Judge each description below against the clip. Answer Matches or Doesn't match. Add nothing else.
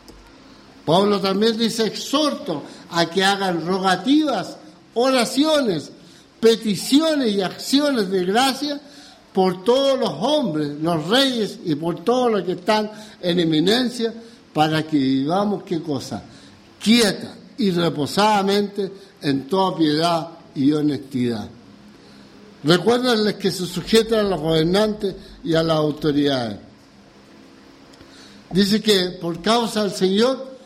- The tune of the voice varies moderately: Doesn't match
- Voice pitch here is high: Matches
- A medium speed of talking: Doesn't match